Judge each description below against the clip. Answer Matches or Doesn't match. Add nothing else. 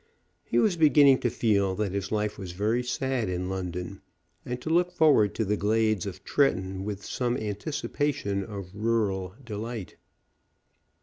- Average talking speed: Matches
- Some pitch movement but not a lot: Matches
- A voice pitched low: Matches